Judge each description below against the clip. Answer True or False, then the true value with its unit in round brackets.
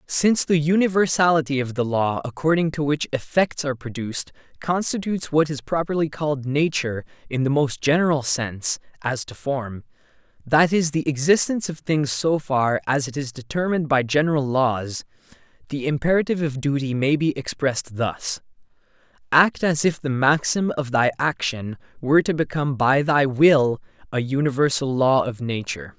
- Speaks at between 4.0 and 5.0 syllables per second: False (5.2 syllables/s)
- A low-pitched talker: False (145 Hz)